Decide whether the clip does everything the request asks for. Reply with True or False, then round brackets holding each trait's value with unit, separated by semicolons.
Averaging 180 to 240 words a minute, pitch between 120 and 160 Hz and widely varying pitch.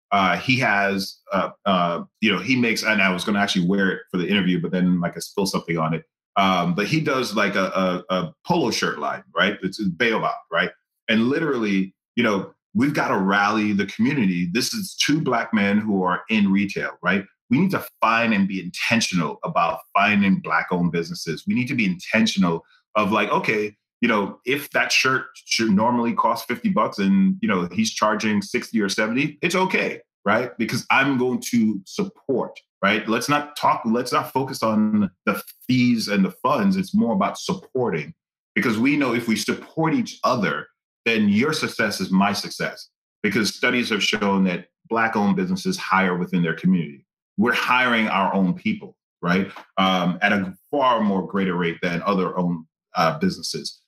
False (190 wpm; 105 Hz; 8.2 semitones)